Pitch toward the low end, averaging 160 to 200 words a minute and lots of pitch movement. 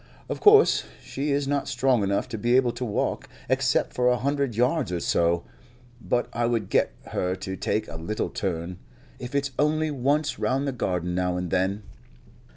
Yes: low, 120 Hz; average, 185 wpm; wide, 6.8 semitones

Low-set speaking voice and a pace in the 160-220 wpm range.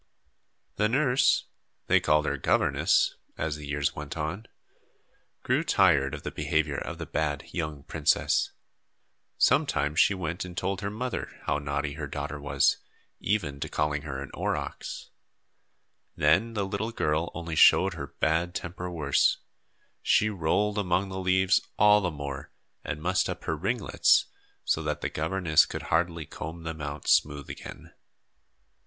No: very low, 80 Hz; average, 150 wpm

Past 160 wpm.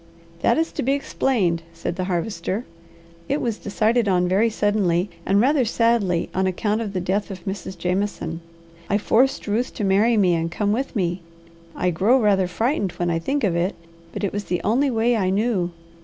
Yes: average, 195 wpm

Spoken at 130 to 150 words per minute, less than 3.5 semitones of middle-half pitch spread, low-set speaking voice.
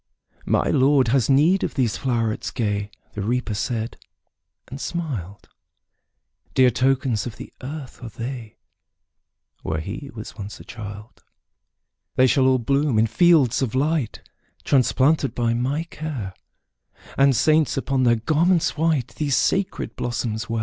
No: average, 140 wpm; average, 4.0 semitones; low, 130 Hz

